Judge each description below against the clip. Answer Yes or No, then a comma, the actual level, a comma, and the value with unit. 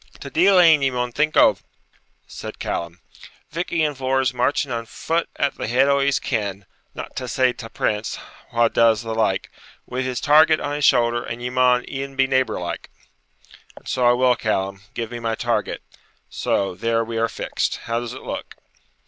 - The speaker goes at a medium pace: Yes, average, 190 wpm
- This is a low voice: Yes, low, 125 Hz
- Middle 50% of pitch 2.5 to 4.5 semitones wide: Yes, average, 3.1 semitones